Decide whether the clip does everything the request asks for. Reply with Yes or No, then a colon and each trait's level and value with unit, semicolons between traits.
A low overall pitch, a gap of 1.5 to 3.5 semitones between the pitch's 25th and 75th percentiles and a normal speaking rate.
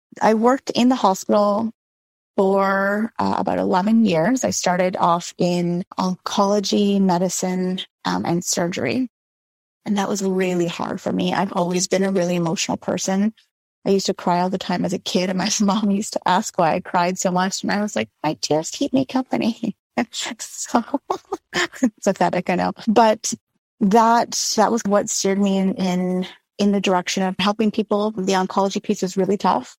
No: high, 195 Hz; average, 3.0 semitones; average, 180 wpm